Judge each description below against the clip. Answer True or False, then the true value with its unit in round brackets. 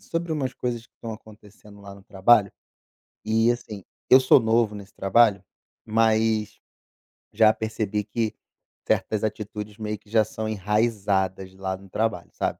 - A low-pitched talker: True (110 Hz)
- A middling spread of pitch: False (1.9 semitones)